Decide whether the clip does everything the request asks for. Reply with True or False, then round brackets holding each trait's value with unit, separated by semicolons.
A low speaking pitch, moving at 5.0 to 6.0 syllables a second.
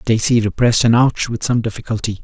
True (115 Hz; 5.9 syllables/s)